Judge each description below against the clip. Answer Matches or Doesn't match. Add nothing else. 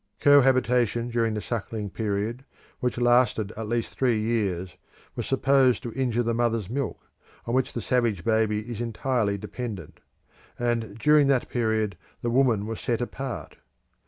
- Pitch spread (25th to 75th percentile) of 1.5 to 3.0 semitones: Matches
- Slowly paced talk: Doesn't match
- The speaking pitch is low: Matches